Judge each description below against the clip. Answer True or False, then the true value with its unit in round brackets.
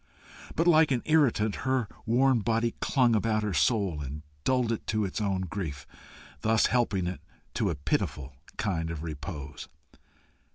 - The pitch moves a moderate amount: False (6.3 semitones)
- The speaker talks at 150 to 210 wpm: True (155 wpm)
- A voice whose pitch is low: True (105 Hz)